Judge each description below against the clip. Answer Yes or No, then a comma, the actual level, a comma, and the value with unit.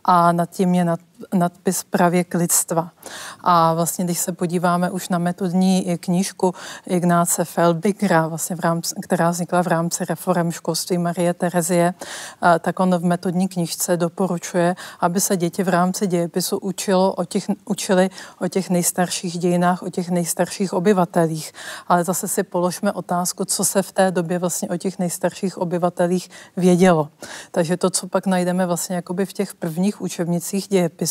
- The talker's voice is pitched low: No, medium, 180 Hz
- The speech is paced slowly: No, average, 150 wpm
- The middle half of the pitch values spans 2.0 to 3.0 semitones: No, narrow, 1.4 semitones